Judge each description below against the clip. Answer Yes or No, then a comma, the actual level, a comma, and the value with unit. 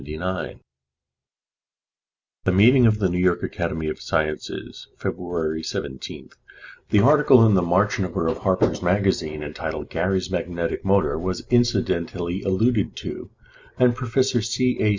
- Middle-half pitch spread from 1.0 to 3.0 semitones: No, average, 4.3 semitones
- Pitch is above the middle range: No, very low, 95 Hz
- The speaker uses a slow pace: Yes, slow, 130 wpm